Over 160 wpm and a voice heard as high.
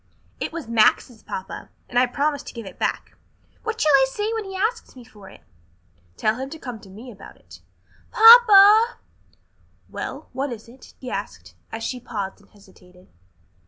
Yes: average, 185 wpm; very high, 250 Hz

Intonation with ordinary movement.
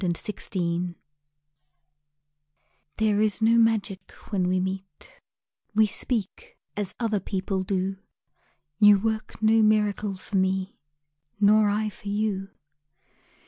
No: narrow, 2.3 semitones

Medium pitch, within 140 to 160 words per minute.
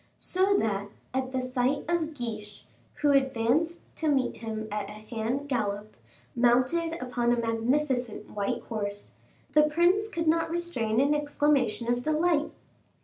No: very high, 255 Hz; average, 145 wpm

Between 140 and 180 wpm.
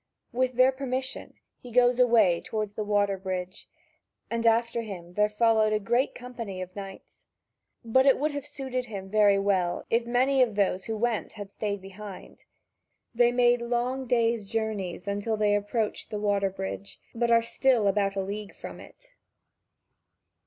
Yes: average, 165 wpm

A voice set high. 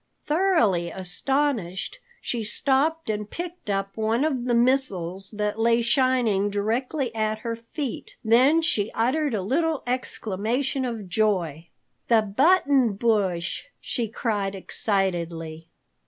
Yes: high, 225 Hz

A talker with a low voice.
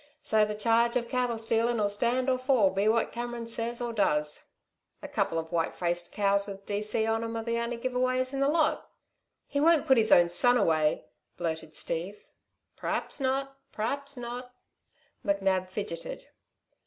No: high, 225 Hz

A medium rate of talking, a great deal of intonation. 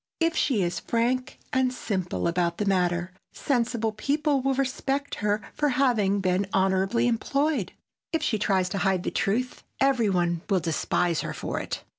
Yes: average, 165 wpm; wide, 5.7 semitones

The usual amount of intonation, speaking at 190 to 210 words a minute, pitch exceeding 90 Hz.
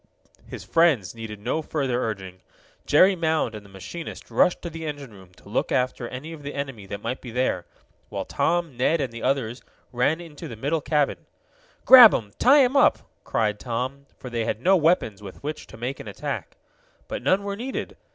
No: wide, 6.3 semitones; average, 200 wpm; low, 135 Hz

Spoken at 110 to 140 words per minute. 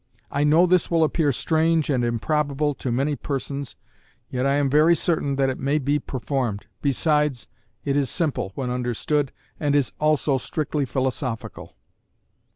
No: average, 150 wpm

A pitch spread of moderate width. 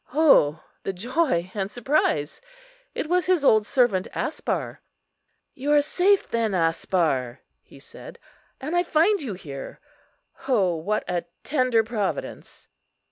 No: wide, 8.7 semitones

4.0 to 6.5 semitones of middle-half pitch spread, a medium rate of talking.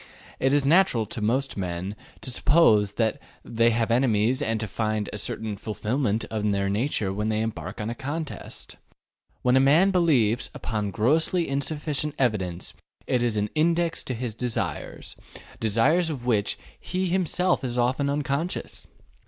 Yes: average, 5.2 semitones; average, 155 wpm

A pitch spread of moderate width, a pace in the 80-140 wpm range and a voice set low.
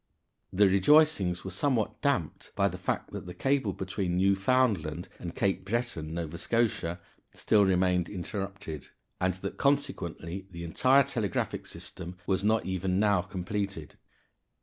Yes: average, 3.3 semitones; slow, 135 wpm; very low, 95 Hz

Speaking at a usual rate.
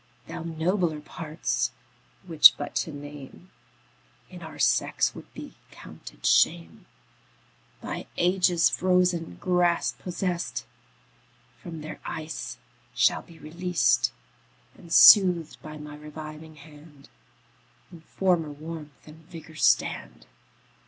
No: slow, 105 wpm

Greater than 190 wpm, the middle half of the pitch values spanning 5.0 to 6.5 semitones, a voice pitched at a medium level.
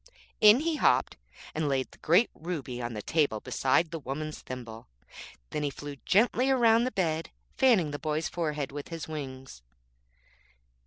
No: average, 160 wpm; average, 5.3 semitones; medium, 155 Hz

